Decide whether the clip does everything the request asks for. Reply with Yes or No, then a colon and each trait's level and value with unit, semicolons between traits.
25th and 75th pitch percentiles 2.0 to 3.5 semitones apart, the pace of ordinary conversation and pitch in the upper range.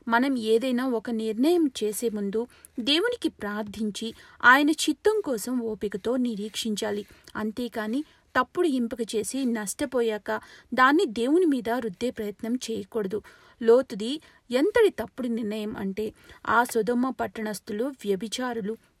Yes: average, 2.9 semitones; average, 105 wpm; high, 235 Hz